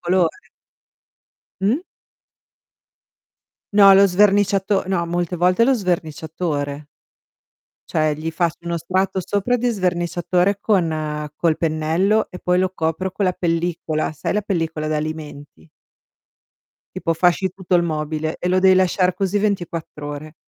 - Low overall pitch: No, medium, 175 Hz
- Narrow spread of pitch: No, average, 3.3 semitones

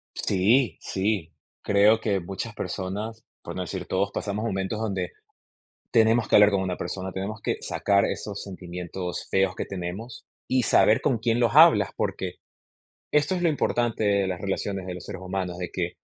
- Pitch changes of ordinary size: Yes, average, 3.1 semitones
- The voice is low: Yes, low, 100 Hz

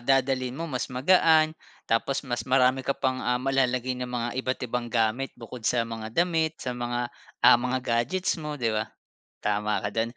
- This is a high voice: No, low, 125 Hz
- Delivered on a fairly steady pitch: Yes, narrow, 2.3 semitones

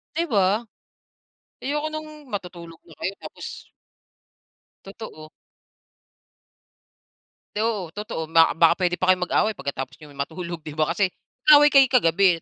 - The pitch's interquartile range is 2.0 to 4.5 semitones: No, average, 5.1 semitones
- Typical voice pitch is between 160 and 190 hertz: Yes, medium, 185 Hz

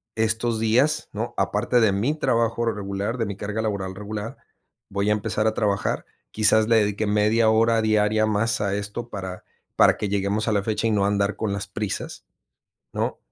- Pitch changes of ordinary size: No, narrow, 1.8 semitones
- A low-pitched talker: Yes, low, 105 Hz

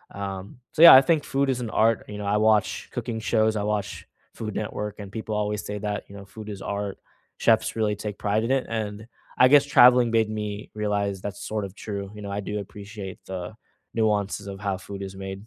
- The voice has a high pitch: No, low, 105 Hz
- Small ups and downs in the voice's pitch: Yes, narrow, 1.7 semitones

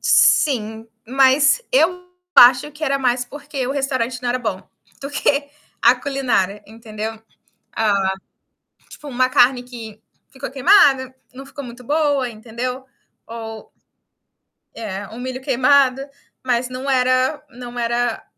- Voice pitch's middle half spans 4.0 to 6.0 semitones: No, average, 2.8 semitones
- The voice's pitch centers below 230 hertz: No, very high, 255 Hz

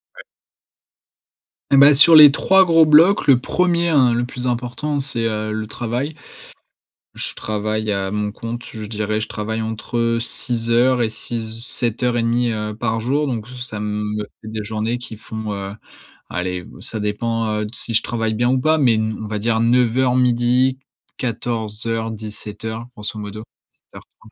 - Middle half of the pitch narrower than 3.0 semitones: Yes, narrow, 2.4 semitones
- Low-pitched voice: Yes, low, 115 Hz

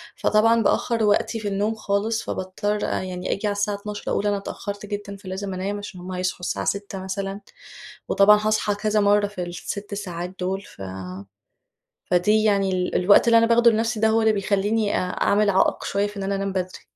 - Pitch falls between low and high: No, high, 205 Hz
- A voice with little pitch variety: Yes, narrow, 1.7 semitones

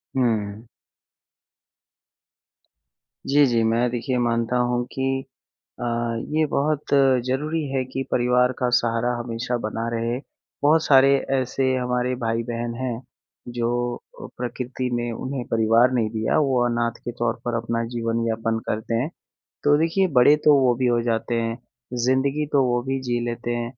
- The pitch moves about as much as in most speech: No, narrow, 2.0 semitones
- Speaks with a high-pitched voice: No, low, 120 Hz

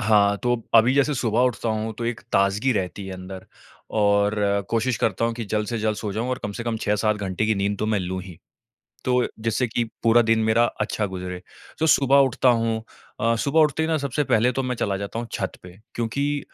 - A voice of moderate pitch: No, low, 110 Hz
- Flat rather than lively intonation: No, average, 3.2 semitones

